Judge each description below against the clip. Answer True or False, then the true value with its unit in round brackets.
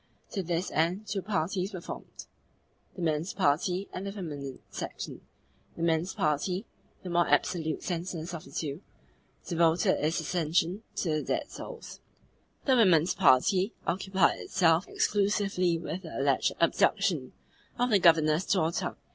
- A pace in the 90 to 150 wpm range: True (140 wpm)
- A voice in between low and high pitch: True (175 Hz)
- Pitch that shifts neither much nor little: True (3.1 semitones)